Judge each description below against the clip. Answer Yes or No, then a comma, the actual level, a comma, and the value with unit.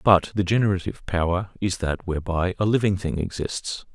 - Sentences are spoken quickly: No, average, 165 wpm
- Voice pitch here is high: No, very low, 95 Hz